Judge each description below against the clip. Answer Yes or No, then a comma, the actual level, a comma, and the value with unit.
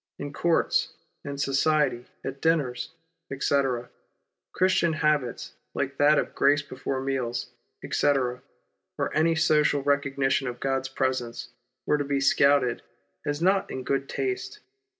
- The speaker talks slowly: Yes, slow, 130 wpm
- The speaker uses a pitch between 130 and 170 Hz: Yes, medium, 140 Hz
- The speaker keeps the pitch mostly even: Yes, narrow, 2.3 semitones